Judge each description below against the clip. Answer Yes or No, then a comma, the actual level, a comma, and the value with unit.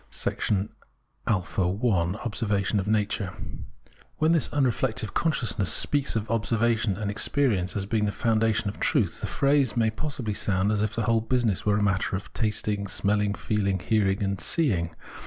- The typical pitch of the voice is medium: No, low, 105 Hz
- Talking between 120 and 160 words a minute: Yes, average, 155 wpm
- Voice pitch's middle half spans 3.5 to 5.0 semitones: No, narrow, 2.4 semitones